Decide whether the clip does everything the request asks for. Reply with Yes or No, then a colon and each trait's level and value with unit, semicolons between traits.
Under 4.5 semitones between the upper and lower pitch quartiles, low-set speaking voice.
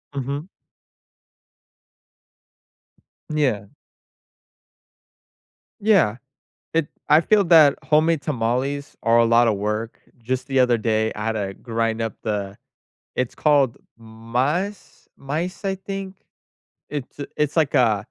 No: average, 5.2 semitones; low, 130 Hz